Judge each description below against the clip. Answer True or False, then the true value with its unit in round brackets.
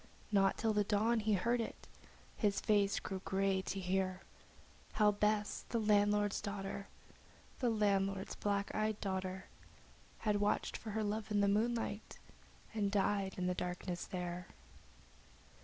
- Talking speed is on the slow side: False (150 wpm)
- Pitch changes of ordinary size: False (1.7 semitones)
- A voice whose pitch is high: True (205 Hz)